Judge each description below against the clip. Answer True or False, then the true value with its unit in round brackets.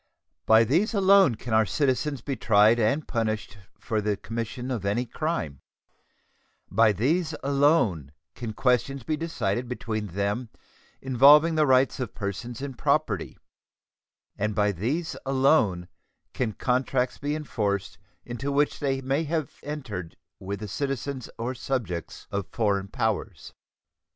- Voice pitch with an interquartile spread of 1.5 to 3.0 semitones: False (4.9 semitones)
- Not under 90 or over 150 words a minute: True (135 wpm)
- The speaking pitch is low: True (120 Hz)